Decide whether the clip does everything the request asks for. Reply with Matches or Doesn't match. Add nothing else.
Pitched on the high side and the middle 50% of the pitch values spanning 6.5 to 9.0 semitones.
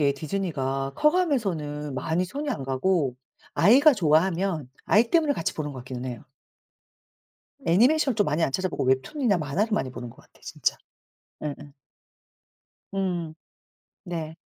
Doesn't match